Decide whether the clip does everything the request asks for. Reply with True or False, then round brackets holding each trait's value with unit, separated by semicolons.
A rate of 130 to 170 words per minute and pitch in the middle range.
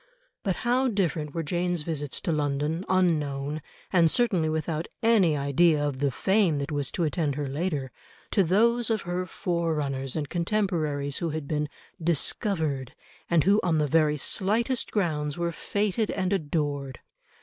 True (155 wpm; 160 Hz)